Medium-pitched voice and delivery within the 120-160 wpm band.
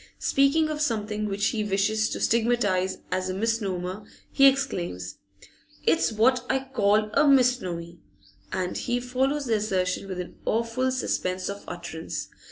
No: high, 215 Hz; average, 145 wpm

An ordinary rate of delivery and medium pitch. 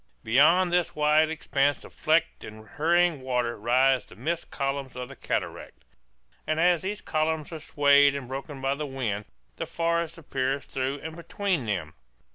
Yes: average, 165 wpm; medium, 145 Hz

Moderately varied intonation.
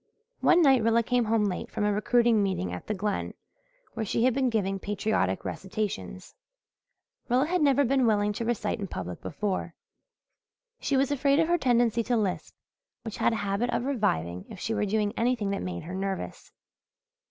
Yes: average, 3.8 semitones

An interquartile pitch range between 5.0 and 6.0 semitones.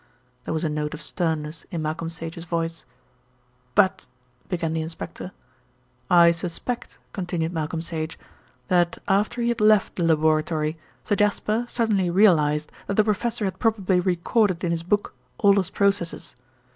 No: average, 3.7 semitones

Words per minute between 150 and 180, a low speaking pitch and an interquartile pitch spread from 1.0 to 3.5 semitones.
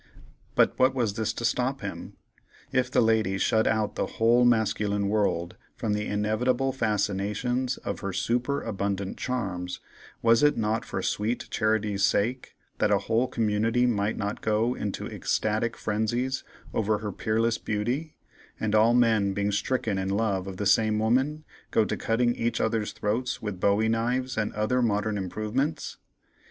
Yes: average, 155 wpm; low, 110 Hz; average, 2.7 semitones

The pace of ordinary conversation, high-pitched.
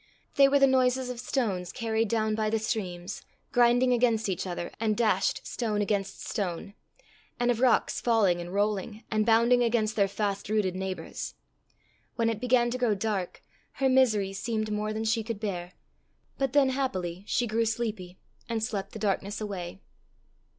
Yes: average, 170 wpm; high, 220 Hz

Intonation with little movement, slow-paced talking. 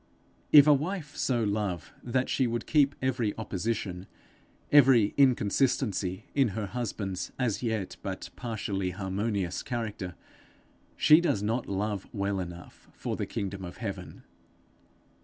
No: average, 4.6 semitones; slow, 130 wpm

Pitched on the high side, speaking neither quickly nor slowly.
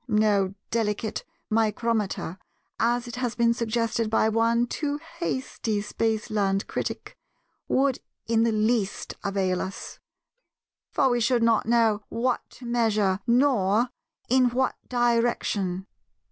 No: high, 230 Hz; slow, 105 wpm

